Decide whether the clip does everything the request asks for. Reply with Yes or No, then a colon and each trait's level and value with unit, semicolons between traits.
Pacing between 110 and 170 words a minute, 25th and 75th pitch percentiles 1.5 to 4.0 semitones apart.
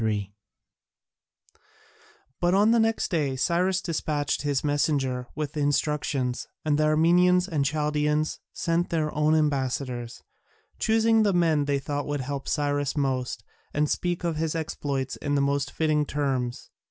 Yes: average, 145 wpm; average, 2.8 semitones